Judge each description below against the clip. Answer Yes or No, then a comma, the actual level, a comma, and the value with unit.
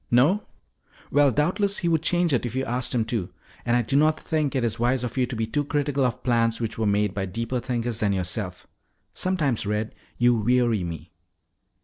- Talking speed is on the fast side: Yes, fast, 210 wpm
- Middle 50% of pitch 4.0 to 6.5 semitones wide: Yes, average, 4.4 semitones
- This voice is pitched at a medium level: No, low, 120 Hz